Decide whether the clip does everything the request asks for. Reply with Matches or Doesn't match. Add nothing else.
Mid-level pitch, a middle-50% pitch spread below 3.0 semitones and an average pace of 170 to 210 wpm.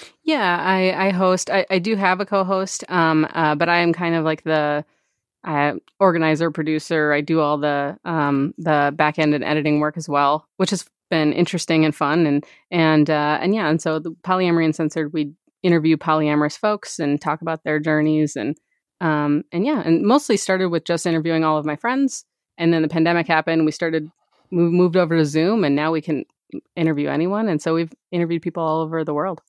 Matches